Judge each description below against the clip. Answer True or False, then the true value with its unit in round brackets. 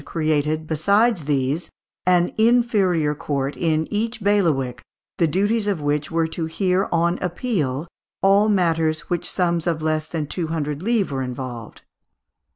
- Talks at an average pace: True (155 wpm)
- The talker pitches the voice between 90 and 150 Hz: False (165 Hz)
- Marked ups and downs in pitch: False (4.5 semitones)